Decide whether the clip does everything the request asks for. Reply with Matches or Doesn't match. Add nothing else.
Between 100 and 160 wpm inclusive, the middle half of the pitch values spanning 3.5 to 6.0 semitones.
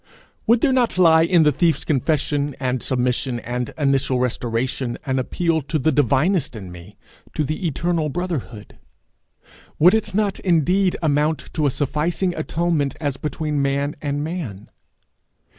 Matches